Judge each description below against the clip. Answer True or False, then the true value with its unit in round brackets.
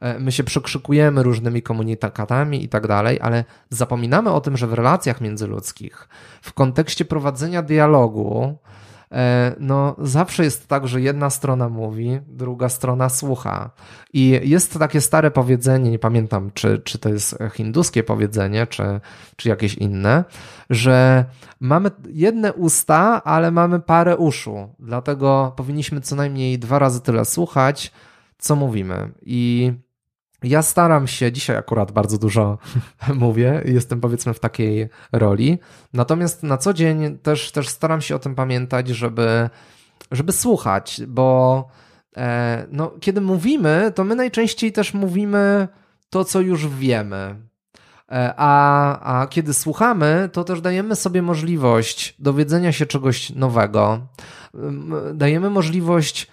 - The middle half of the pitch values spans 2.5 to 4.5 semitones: False (5.0 semitones)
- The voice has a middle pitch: False (130 Hz)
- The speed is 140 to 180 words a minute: False (130 wpm)